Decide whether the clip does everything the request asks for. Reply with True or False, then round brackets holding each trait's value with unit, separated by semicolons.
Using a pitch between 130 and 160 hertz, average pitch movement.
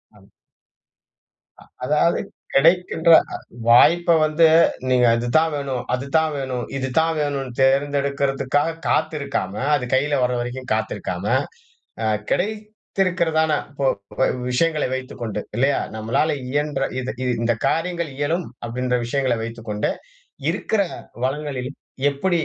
True (140 Hz; 3.9 semitones)